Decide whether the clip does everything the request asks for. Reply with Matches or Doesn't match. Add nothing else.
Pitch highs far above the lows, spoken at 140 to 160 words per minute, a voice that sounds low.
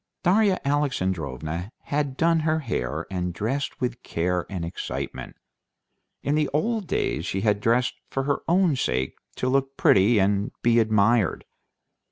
Matches